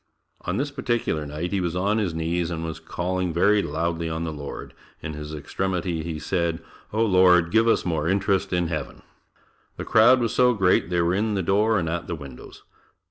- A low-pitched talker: Yes, very low, 90 Hz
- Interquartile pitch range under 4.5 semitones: Yes, average, 3.4 semitones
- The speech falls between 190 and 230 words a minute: Yes, average, 200 wpm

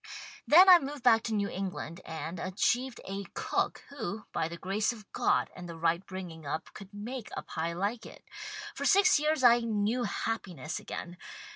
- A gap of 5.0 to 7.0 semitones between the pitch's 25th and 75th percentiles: Yes, wide, 5.6 semitones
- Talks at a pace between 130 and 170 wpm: No, average, 185 wpm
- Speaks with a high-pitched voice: Yes, high, 205 Hz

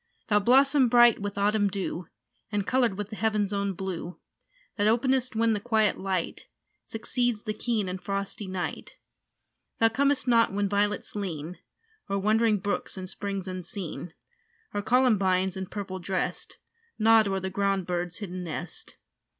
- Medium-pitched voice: No, high, 205 Hz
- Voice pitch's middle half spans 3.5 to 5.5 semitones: No, average, 2.8 semitones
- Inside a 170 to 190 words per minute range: No, average, 150 wpm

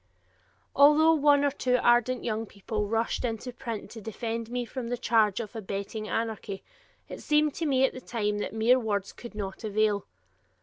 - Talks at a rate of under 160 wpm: No, average, 180 wpm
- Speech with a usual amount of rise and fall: Yes, average, 3.1 semitones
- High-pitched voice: Yes, high, 230 Hz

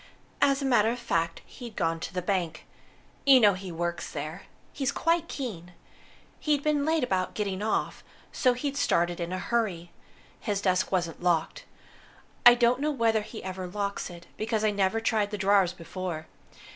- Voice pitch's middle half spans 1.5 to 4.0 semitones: No, average, 5.3 semitones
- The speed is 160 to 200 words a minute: Yes, average, 175 wpm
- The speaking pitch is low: No, high, 200 Hz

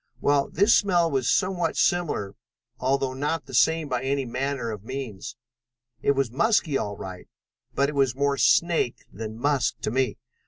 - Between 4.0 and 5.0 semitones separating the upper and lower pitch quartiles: No, average, 3.6 semitones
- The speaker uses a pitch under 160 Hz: Yes, low, 135 Hz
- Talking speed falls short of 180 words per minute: Yes, average, 165 wpm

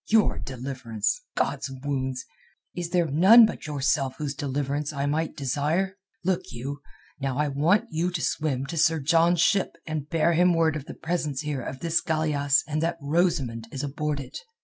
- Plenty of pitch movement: No, average, 3.3 semitones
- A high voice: No, medium, 150 Hz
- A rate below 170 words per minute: No, average, 175 wpm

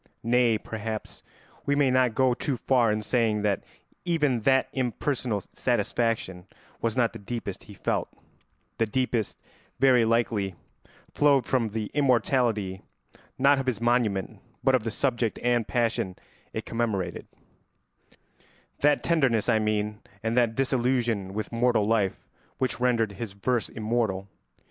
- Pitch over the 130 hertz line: No, low, 115 Hz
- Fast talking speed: No, slow, 135 wpm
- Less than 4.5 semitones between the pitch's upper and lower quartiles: Yes, average, 3.0 semitones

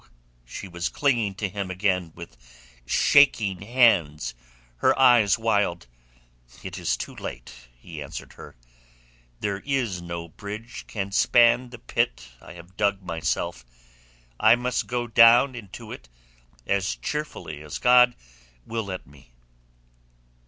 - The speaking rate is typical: No, slow, 130 wpm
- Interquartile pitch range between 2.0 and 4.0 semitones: No, wide, 5.6 semitones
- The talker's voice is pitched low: Yes, low, 100 Hz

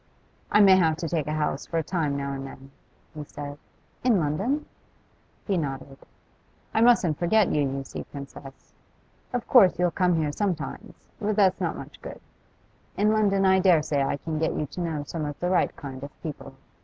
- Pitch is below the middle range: No, medium, 160 Hz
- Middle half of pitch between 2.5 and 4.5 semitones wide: No, average, 4.9 semitones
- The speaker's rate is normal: Yes, average, 195 wpm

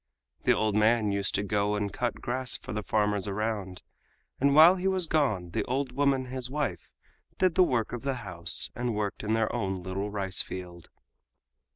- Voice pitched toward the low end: Yes, low, 110 Hz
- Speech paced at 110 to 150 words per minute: No, average, 190 wpm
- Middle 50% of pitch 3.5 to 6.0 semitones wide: Yes, average, 4.7 semitones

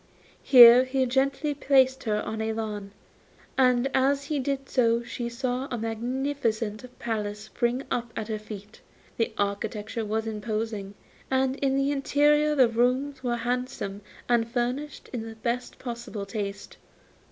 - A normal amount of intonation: Yes, average, 3.2 semitones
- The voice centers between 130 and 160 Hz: No, high, 240 Hz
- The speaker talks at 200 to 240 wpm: No, average, 145 wpm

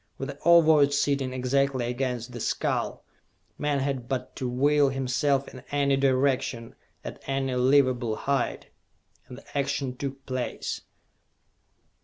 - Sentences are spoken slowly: Yes, slow, 130 wpm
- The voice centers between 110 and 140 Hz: Yes, low, 135 Hz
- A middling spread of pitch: No, narrow, 1.7 semitones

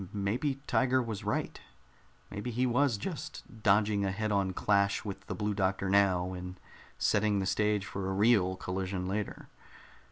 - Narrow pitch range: Yes, narrow, 2.2 semitones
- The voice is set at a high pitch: No, low, 100 Hz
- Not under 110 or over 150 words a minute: No, average, 160 wpm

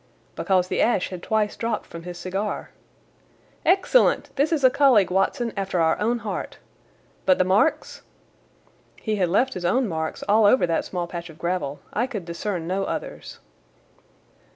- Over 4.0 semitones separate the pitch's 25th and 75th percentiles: Yes, average, 4.6 semitones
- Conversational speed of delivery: Yes, average, 165 wpm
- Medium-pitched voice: No, high, 195 Hz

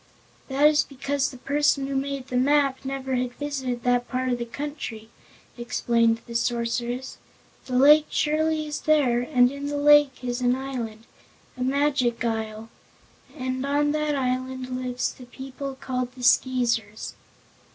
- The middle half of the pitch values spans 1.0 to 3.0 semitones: Yes, narrow, 2.5 semitones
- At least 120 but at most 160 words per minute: Yes, average, 150 wpm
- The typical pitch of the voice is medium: No, very high, 260 Hz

